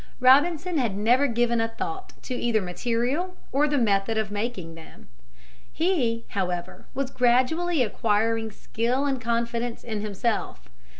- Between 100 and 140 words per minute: Yes, slow, 135 wpm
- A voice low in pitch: No, high, 235 Hz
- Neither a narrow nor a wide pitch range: Yes, average, 3.7 semitones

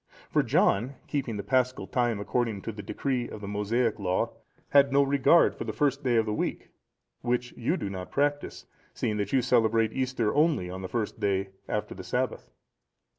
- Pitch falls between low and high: No, low, 120 Hz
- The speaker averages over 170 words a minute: Yes, average, 190 wpm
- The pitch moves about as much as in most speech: Yes, average, 4.4 semitones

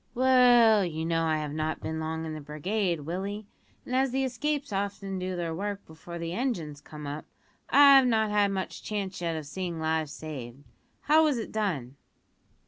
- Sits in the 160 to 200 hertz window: Yes, medium, 185 Hz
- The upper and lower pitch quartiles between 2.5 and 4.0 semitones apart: No, wide, 5.6 semitones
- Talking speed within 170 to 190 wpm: Yes, average, 185 wpm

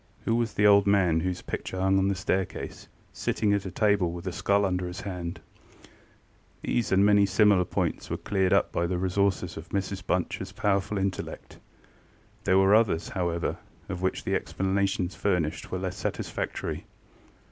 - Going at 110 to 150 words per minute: No, average, 170 wpm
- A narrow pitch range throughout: Yes, narrow, 1.9 semitones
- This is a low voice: Yes, very low, 95 Hz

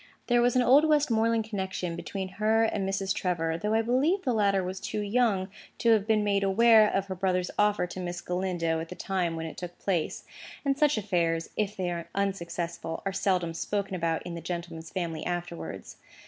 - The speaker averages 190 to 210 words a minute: Yes, average, 200 wpm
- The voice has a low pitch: No, high, 190 Hz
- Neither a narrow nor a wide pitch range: Yes, average, 3.7 semitones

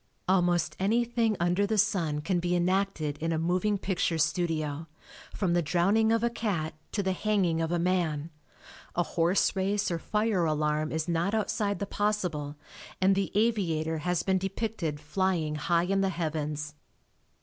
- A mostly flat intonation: No, average, 3.7 semitones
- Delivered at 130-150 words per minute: No, average, 160 wpm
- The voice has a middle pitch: Yes, medium, 175 Hz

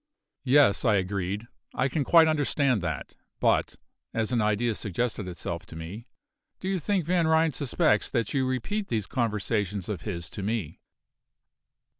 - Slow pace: No, average, 155 wpm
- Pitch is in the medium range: No, low, 115 Hz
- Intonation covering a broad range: Yes, wide, 6.0 semitones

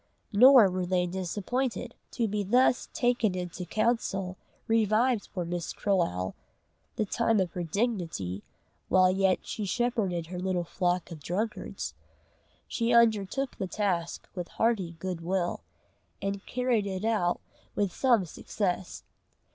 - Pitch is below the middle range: No, high, 195 Hz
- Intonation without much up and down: No, average, 4.2 semitones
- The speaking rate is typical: No, slow, 130 wpm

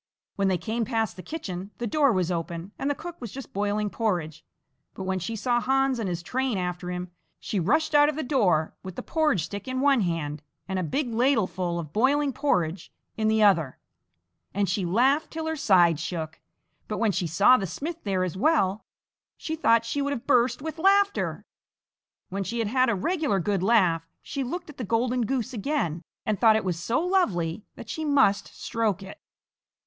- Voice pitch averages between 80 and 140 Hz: No, high, 215 Hz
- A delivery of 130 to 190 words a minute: No, fast, 205 wpm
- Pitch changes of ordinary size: No, wide, 6.7 semitones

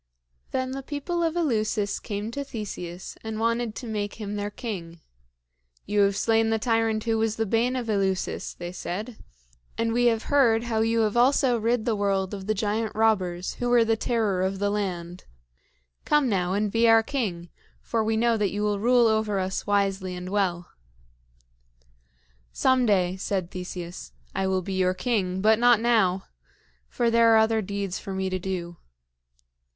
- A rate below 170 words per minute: No, average, 180 wpm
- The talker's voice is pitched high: Yes, high, 215 Hz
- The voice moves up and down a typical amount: Yes, average, 3.3 semitones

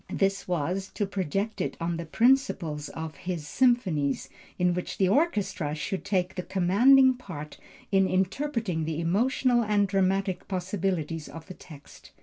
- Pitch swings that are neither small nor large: Yes, average, 3.7 semitones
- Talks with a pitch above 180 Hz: Yes, high, 190 Hz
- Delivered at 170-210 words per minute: No, average, 145 wpm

